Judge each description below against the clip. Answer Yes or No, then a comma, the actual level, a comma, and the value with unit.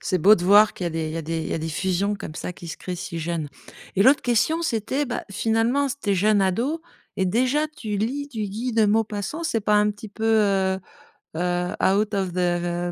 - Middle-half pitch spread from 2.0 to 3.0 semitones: No, average, 4.0 semitones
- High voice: Yes, high, 205 Hz